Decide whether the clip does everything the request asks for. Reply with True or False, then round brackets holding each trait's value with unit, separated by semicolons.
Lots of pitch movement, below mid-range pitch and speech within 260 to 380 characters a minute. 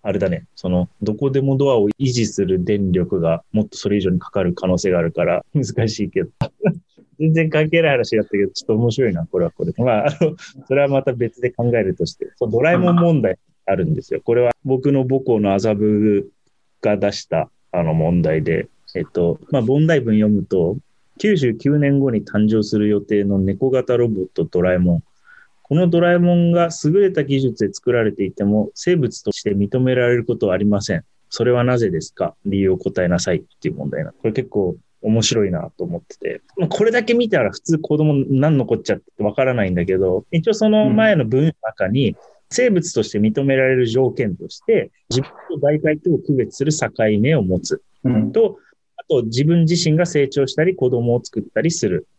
True (7.3 semitones; 130 Hz; 365 characters per minute)